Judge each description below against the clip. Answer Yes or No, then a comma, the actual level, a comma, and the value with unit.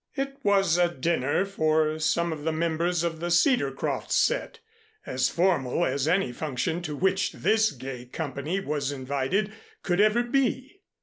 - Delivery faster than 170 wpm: No, average, 150 wpm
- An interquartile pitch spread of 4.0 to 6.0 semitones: Yes, wide, 5.4 semitones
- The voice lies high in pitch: No, medium, 170 Hz